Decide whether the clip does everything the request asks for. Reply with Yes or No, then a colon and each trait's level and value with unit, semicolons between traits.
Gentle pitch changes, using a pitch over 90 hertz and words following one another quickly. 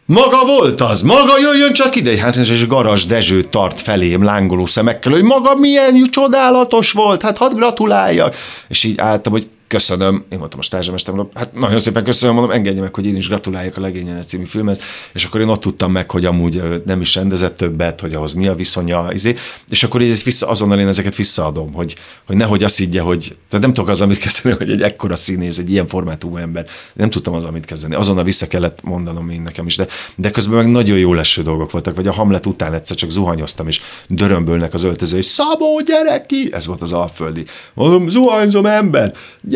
No: average, 5.1 semitones; low, 100 Hz; fast, 205 wpm